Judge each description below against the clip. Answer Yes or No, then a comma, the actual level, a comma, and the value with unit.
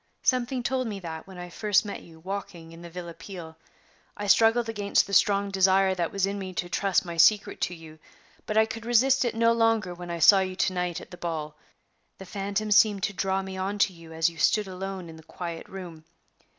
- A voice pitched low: No, high, 190 Hz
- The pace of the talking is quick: Yes, fast, 230 wpm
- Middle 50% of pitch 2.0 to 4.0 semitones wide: Yes, average, 3.3 semitones